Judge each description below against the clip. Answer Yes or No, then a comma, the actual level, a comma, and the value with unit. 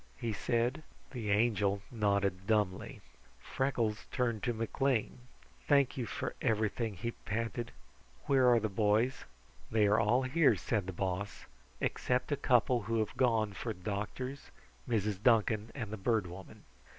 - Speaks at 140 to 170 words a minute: Yes, average, 145 wpm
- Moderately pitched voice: No, low, 110 Hz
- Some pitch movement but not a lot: Yes, average, 3.1 semitones